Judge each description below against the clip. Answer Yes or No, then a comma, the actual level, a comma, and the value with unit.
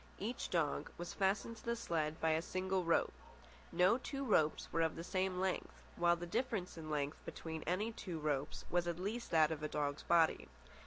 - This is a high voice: No, medium, 175 Hz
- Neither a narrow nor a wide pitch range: Yes, average, 3.2 semitones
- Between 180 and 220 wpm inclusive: Yes, average, 200 wpm